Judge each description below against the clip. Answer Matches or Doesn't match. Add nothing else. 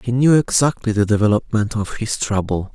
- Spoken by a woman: Doesn't match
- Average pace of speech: Matches